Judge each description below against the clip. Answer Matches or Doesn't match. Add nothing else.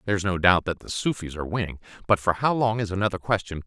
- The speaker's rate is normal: Doesn't match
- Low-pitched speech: Matches